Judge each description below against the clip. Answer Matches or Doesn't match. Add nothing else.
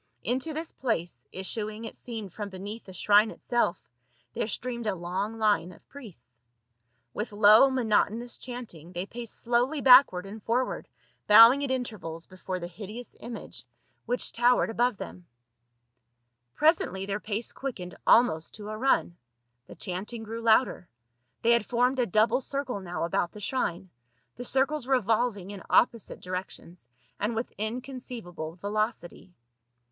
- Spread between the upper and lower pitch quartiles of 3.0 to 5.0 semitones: Matches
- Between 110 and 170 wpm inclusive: Matches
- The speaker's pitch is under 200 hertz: Doesn't match